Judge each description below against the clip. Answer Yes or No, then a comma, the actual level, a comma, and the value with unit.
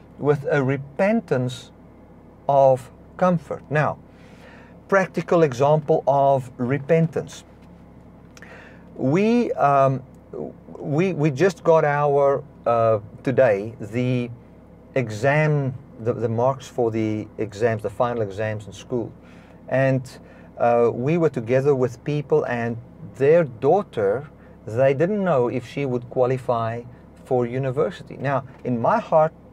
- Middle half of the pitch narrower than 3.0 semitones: No, average, 4.3 semitones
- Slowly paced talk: Yes, slow, 110 wpm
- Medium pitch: No, low, 130 Hz